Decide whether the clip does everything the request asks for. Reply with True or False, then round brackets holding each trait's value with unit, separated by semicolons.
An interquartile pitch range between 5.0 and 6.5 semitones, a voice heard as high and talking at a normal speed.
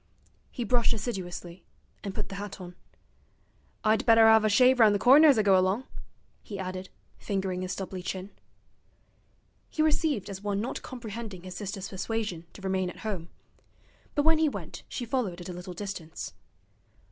False (3.8 semitones; 200 Hz; 170 wpm)